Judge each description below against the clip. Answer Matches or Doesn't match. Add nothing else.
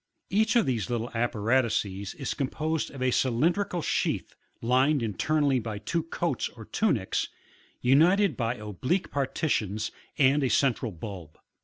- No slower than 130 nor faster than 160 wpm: Matches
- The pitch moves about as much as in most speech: Doesn't match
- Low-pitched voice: Matches